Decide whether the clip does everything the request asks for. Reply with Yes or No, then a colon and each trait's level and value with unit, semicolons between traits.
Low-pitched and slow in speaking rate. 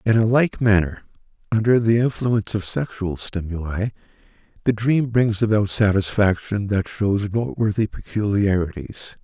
Yes: low, 105 Hz; slow, 125 wpm